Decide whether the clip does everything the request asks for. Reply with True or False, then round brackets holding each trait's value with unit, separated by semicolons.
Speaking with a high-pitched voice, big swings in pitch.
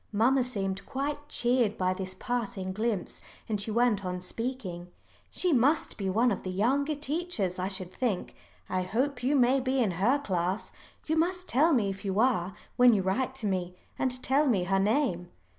True (225 Hz; 5.7 semitones)